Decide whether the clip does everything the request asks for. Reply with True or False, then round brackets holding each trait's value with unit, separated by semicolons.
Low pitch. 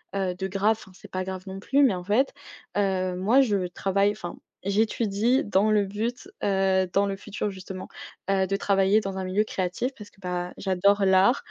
False (195 Hz)